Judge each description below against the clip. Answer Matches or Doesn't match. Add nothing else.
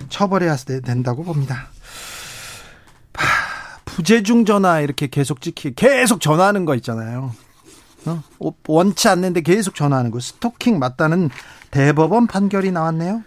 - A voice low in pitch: Doesn't match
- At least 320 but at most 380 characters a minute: Doesn't match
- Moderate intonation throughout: Doesn't match